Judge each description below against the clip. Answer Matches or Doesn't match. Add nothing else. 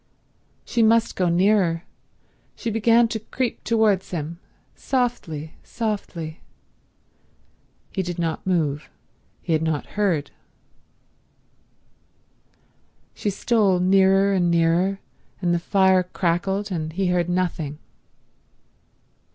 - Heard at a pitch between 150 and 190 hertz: Matches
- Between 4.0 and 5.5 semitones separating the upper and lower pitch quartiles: Doesn't match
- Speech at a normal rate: Doesn't match